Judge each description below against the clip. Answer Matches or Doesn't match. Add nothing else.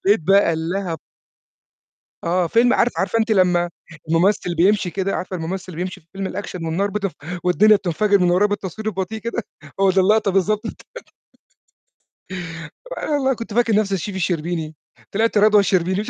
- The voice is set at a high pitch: Matches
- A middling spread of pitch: Matches